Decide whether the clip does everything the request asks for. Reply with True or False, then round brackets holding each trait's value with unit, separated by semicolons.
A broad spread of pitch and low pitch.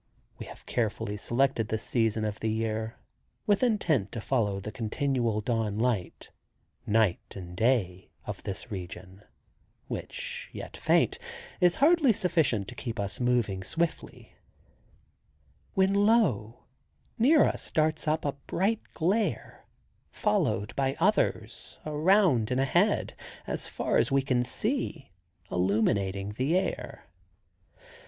True (8.4 semitones; 125 Hz)